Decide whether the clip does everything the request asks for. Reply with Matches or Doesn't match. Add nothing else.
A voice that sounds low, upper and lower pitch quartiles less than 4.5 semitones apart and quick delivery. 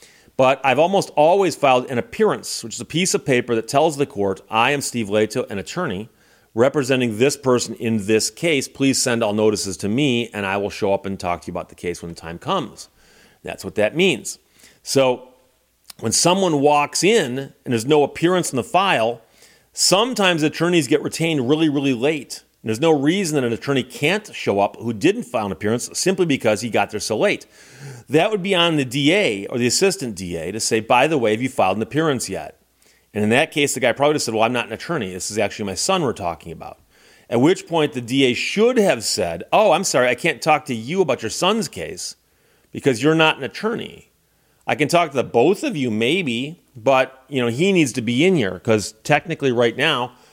Doesn't match